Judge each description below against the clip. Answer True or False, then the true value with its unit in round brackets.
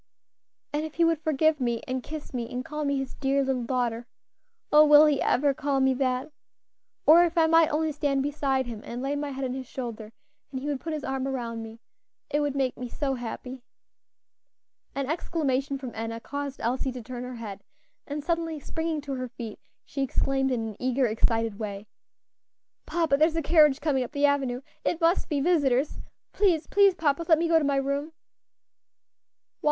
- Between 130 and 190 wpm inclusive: False (200 wpm)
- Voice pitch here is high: True (275 Hz)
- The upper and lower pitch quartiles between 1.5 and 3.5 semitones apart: True (3.2 semitones)